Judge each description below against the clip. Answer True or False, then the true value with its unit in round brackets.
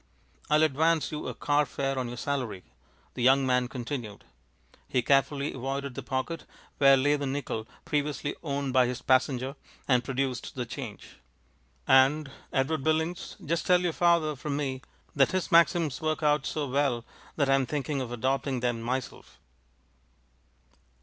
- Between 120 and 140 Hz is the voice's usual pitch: True (135 Hz)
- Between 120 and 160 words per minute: True (155 wpm)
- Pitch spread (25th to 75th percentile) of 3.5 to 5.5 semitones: False (2.6 semitones)